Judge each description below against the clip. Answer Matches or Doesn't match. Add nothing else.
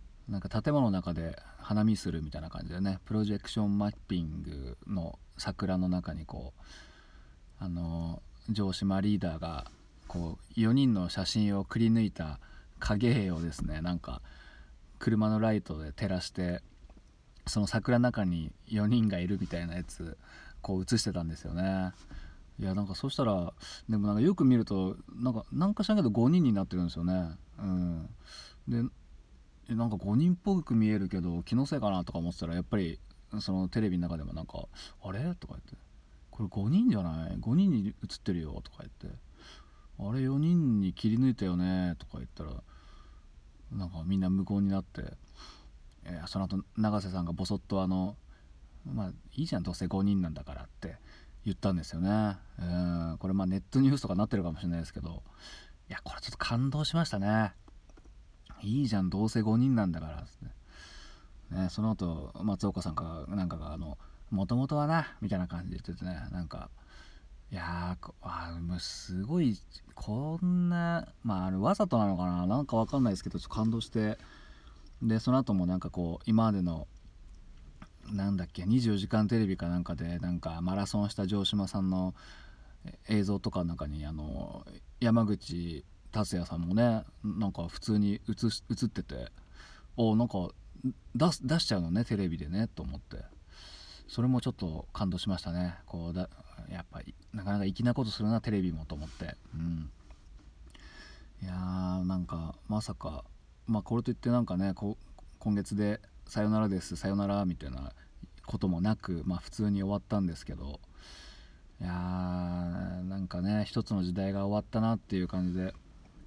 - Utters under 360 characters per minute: Matches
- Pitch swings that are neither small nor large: Matches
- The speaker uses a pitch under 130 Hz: Matches